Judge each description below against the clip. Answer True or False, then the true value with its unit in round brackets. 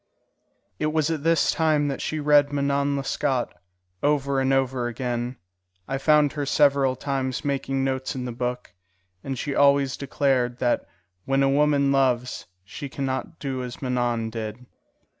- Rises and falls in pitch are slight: True (2.1 semitones)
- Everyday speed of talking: True (160 wpm)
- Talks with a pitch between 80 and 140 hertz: True (135 Hz)